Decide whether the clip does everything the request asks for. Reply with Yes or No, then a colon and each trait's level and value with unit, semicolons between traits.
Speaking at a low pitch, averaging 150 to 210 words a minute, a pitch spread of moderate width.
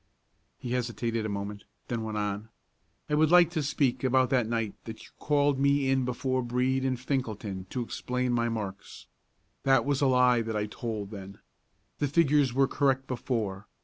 Yes: low, 125 Hz; average, 180 wpm; average, 3.3 semitones